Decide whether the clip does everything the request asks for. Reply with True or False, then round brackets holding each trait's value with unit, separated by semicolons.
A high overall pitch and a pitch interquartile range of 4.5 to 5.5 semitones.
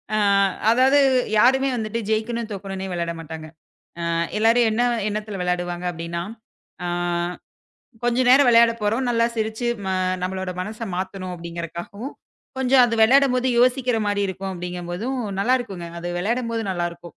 True (215 Hz; 5.2 semitones)